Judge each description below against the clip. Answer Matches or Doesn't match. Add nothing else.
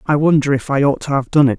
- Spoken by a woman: Matches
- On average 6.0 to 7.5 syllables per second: Matches